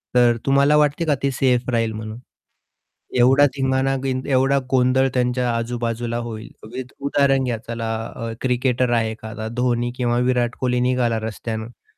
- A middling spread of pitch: No, narrow, 2.2 semitones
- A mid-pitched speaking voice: No, low, 125 Hz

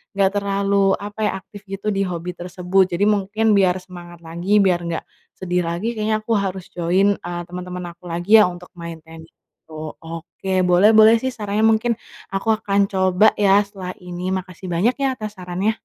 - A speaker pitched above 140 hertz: Yes, high, 190 Hz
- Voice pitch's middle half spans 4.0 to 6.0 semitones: No, average, 2.7 semitones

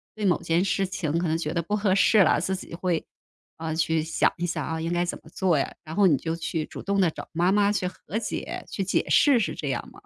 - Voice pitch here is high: No, medium, 175 Hz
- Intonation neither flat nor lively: Yes, average, 3.2 semitones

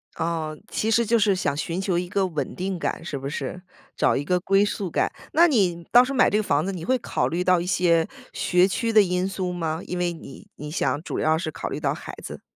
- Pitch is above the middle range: No, medium, 180 Hz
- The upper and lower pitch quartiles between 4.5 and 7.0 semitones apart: No, average, 3.4 semitones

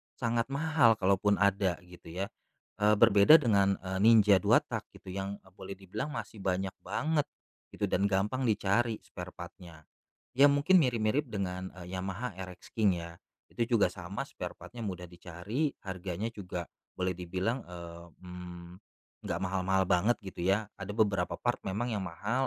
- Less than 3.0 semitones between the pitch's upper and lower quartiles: No, average, 3.8 semitones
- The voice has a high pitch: No, low, 100 Hz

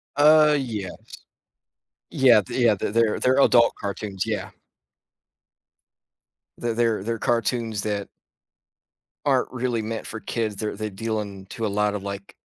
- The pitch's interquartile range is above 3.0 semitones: No, narrow, 2.6 semitones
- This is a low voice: Yes, low, 110 Hz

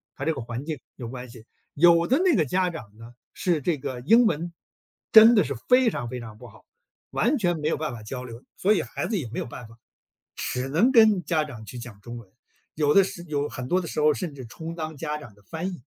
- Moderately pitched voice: Yes, medium, 150 Hz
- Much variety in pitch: Yes, wide, 6.3 semitones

